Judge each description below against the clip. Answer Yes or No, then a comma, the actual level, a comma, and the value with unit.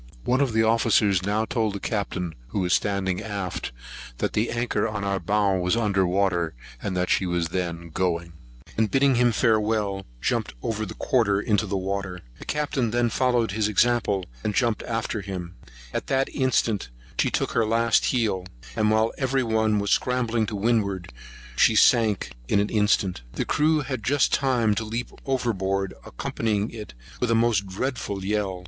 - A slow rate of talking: No, average, 175 wpm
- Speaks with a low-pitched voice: Yes, low, 105 Hz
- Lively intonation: No, average, 3.2 semitones